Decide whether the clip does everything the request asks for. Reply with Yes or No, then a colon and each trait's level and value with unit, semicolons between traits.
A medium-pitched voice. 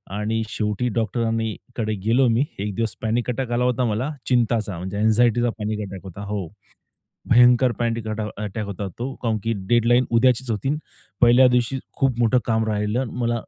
No: low, 115 Hz